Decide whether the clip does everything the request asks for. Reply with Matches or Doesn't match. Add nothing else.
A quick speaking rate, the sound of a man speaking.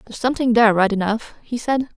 Doesn't match